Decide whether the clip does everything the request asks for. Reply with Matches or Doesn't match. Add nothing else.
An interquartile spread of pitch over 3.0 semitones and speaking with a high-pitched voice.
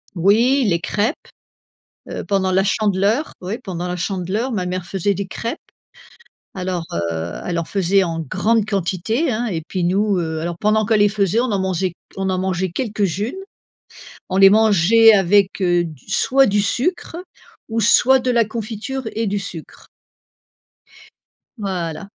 Matches